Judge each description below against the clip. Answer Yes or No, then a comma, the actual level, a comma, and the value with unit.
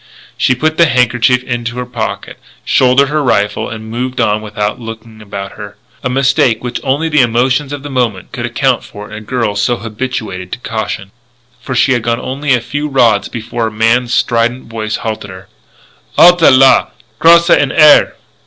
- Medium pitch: No, low, 120 Hz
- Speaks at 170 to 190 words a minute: Yes, average, 180 wpm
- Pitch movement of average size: Yes, average, 3.2 semitones